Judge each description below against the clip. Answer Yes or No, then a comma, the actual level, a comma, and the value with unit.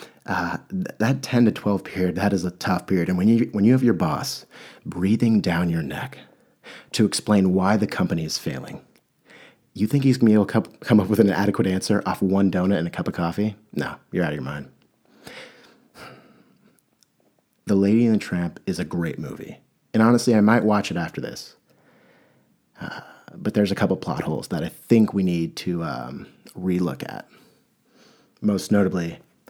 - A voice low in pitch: Yes, low, 100 Hz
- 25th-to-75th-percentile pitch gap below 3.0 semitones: No, average, 3.4 semitones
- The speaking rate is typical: Yes, average, 185 wpm